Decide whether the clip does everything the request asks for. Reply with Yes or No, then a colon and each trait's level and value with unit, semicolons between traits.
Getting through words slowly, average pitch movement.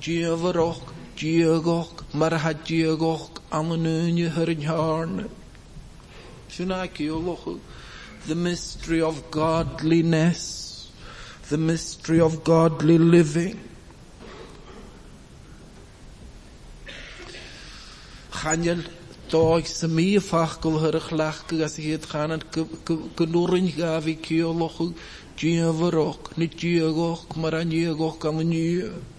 No: slow, 90 wpm; narrow, 0.8 semitones